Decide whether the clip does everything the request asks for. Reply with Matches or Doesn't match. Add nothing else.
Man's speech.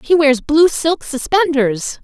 Doesn't match